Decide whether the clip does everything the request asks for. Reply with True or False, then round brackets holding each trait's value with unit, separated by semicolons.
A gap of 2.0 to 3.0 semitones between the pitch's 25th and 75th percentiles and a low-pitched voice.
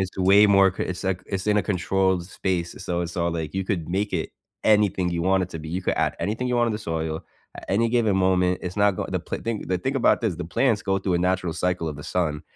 True (2.7 semitones; 95 Hz)